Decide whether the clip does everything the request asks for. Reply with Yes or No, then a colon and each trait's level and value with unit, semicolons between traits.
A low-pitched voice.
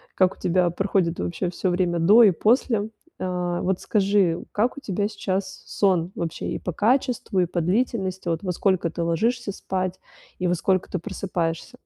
No: medium, 185 Hz